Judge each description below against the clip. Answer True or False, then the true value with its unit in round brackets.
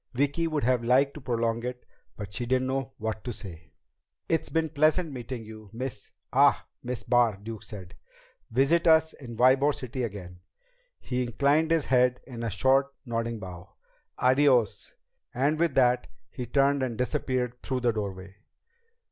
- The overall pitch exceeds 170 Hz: False (125 Hz)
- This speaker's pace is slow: False (160 wpm)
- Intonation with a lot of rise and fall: False (3.4 semitones)